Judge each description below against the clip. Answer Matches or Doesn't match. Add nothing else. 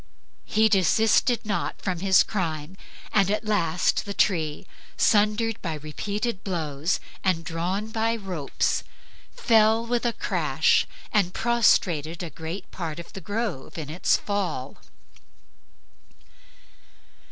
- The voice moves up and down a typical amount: Matches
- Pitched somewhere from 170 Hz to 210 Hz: Matches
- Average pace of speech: Doesn't match